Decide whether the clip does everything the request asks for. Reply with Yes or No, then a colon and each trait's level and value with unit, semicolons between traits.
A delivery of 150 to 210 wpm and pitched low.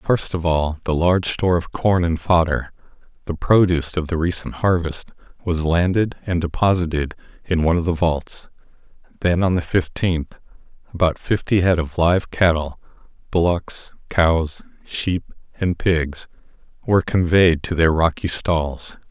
No: average, 140 wpm; very low, 85 Hz